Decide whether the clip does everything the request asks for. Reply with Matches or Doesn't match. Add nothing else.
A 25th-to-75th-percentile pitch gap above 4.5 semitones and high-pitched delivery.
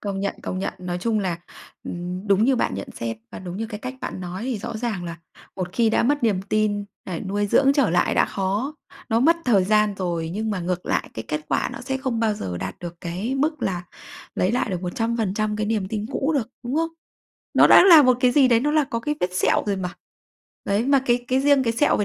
Matches